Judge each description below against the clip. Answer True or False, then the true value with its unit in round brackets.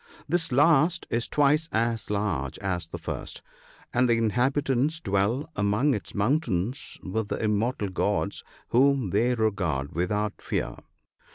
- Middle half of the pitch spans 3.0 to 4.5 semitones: False (5.5 semitones)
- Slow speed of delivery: True (130 wpm)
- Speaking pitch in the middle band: False (115 Hz)